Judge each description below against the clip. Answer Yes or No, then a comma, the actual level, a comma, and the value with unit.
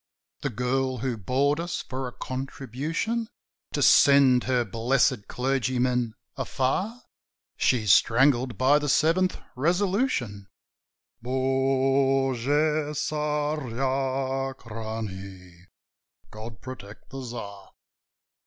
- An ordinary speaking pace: No, slow, 85 wpm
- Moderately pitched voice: No, low, 130 Hz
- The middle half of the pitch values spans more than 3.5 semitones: No, average, 3.2 semitones